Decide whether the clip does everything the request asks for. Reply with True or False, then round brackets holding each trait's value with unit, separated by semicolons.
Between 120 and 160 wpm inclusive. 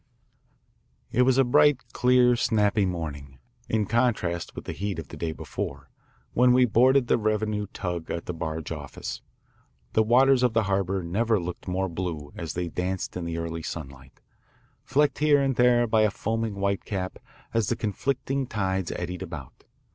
False (170 wpm)